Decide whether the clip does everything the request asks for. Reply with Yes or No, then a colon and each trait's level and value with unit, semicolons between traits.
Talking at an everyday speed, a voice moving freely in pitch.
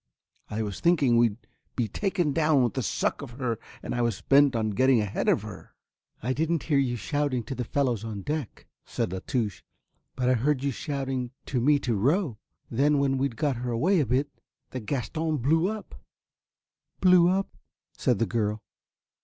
No: average, 185 wpm; average, 4.0 semitones